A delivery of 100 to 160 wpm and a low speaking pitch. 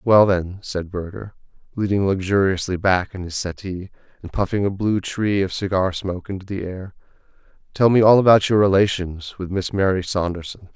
No: average, 175 wpm; very low, 95 Hz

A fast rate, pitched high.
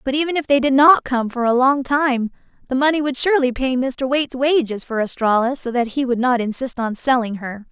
Yes: fast, 235 wpm; very high, 260 Hz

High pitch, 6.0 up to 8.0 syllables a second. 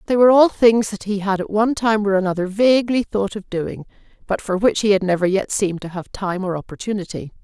Yes: high, 200 Hz; 6.1 syllables/s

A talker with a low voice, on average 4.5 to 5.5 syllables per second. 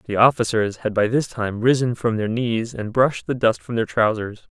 Yes: low, 115 Hz; 5.1 syllables/s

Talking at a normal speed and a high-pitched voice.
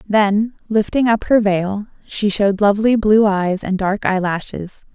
Yes: average, 160 wpm; high, 205 Hz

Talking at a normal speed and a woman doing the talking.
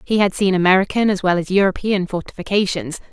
Yes: average, 175 wpm; female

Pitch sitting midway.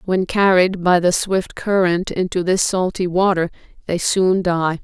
Yes: medium, 180 Hz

